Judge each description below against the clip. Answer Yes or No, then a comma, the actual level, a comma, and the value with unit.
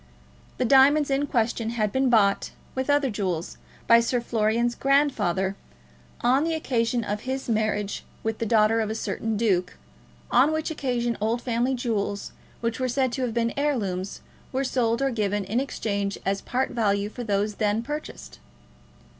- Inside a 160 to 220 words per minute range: Yes, average, 165 wpm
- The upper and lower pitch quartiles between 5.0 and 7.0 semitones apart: No, average, 3.8 semitones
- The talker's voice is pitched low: No, high, 230 Hz